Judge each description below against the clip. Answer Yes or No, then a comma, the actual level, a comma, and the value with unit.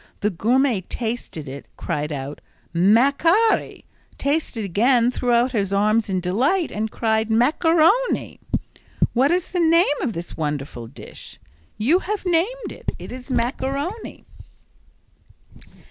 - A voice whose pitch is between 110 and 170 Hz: No, high, 245 Hz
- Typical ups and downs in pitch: No, wide, 8.2 semitones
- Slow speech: Yes, slow, 125 wpm